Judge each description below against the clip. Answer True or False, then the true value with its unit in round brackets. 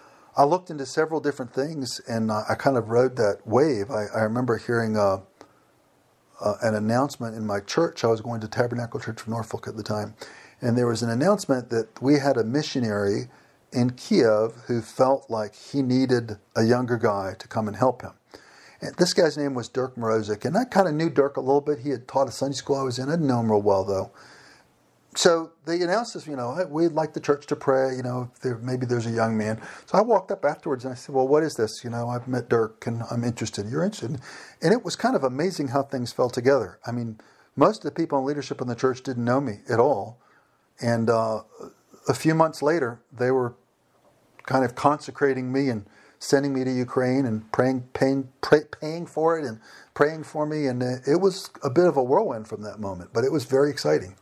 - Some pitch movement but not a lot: True (3.7 semitones)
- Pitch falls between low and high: False (130 Hz)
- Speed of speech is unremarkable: False (225 wpm)